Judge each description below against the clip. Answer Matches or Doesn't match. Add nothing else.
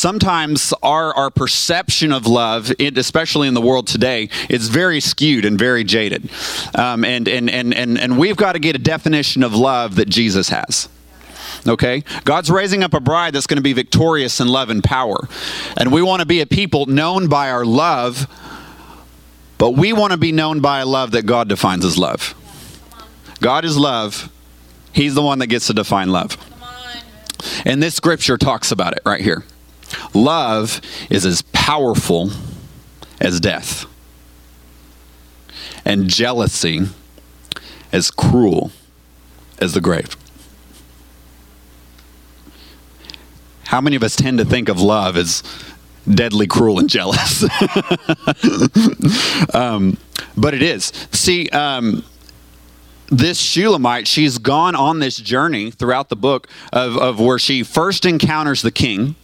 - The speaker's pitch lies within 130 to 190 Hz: Doesn't match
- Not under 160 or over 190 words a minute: Doesn't match